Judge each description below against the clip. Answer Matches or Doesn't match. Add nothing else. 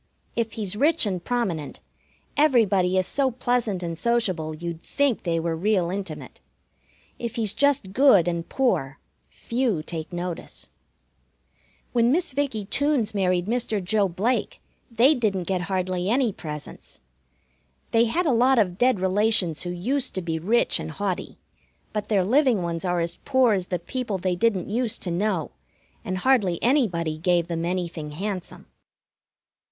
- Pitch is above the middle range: Matches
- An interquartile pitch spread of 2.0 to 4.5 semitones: Doesn't match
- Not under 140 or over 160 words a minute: Matches